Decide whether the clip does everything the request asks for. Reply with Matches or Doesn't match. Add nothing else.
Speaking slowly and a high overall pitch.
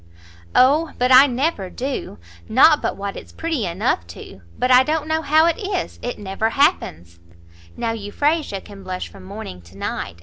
Doesn't match